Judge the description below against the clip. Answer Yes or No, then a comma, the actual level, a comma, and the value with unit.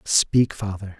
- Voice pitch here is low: Yes, very low, 95 Hz